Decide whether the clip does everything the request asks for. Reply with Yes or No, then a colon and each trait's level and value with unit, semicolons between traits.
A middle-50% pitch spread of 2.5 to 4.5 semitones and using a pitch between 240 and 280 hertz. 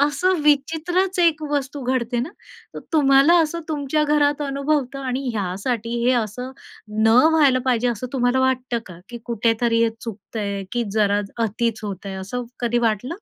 Yes: average, 4.1 semitones; very high, 250 Hz